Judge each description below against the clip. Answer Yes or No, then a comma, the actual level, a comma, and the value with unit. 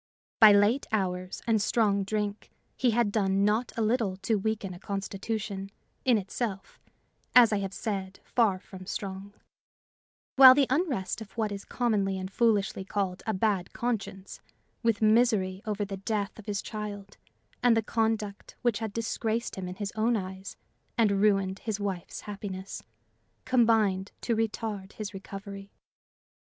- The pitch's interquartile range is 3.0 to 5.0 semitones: No, narrow, 2.5 semitones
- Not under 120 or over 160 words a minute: Yes, average, 150 wpm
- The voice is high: Yes, high, 205 Hz